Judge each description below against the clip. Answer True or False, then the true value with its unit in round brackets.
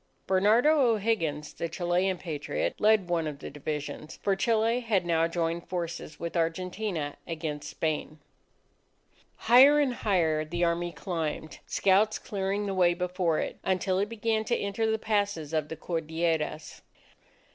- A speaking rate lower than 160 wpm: True (145 wpm)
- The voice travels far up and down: False (4.3 semitones)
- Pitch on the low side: False (175 Hz)